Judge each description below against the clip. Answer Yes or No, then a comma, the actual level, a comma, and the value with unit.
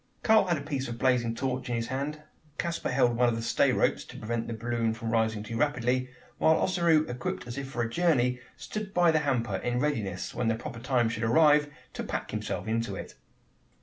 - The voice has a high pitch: No, low, 125 Hz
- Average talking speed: No, fast, 215 wpm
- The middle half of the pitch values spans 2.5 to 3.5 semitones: No, average, 4.3 semitones